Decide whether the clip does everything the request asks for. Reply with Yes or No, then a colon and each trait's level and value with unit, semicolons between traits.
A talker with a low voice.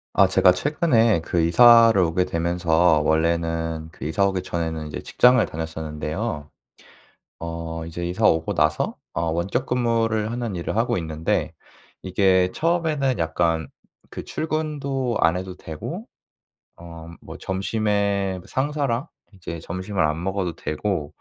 Yes: very low, 90 Hz